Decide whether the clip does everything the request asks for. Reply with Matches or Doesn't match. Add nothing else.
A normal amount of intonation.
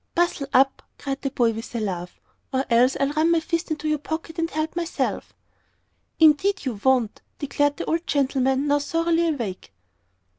Matches